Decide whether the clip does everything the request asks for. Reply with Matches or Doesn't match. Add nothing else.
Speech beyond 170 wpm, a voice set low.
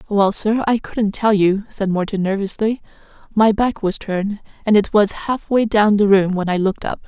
Doesn't match